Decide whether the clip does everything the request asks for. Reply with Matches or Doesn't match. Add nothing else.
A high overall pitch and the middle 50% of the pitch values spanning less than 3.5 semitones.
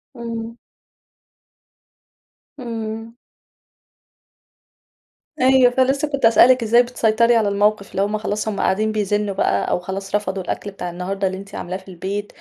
Matches